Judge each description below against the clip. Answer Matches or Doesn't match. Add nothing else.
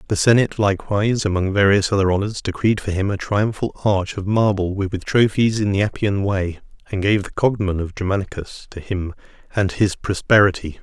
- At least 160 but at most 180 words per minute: Matches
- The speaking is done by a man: Matches